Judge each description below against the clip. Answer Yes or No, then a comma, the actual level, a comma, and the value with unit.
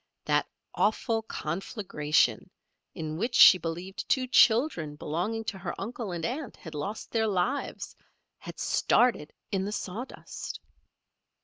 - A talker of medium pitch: No, high, 195 Hz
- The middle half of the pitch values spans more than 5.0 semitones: Yes, wide, 5.6 semitones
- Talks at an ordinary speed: No, slow, 125 wpm